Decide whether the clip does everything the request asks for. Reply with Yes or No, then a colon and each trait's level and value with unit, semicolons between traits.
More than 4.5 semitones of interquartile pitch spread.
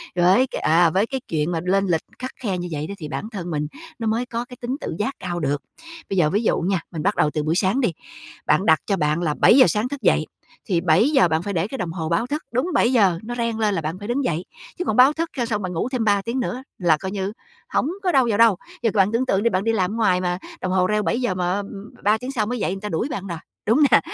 Yes: average, 5.1 semitones